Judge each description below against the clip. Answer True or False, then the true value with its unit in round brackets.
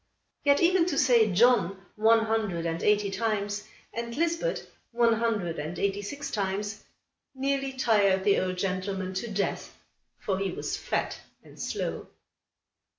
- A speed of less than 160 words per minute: True (145 wpm)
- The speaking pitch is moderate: False (210 Hz)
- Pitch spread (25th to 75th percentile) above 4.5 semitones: False (3.7 semitones)